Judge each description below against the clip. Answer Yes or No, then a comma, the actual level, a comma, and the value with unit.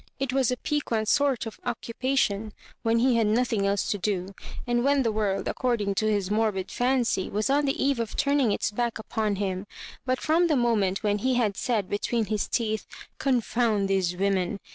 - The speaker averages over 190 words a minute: Yes, average, 200 wpm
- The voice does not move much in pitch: No, average, 3.7 semitones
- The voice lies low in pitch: No, high, 225 Hz